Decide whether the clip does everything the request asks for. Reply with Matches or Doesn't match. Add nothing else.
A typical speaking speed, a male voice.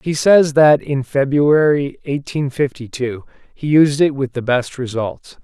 Matches